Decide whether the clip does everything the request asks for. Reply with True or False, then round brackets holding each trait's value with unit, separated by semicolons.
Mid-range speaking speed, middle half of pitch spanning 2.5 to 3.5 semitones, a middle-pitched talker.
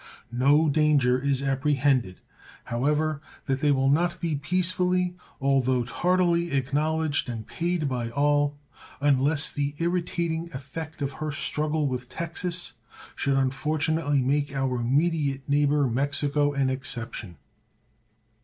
False (115 wpm; 2.9 semitones; 145 Hz)